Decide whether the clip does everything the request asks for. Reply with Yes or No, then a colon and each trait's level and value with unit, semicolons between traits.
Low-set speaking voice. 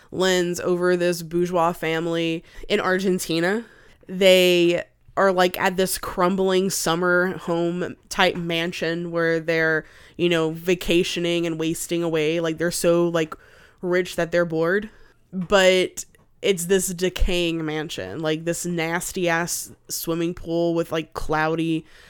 No: medium, 170 Hz